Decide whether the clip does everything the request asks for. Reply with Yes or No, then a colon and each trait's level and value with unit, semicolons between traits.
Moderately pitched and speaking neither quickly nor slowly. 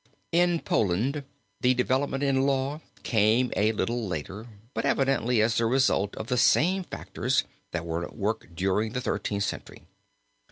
No: low, 120 Hz; average, 155 wpm